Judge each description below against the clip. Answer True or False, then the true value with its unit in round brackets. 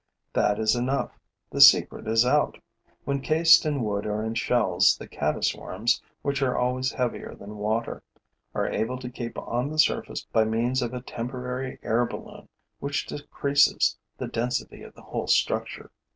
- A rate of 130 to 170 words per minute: True (165 wpm)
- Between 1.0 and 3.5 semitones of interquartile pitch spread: True (3.0 semitones)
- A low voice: True (125 Hz)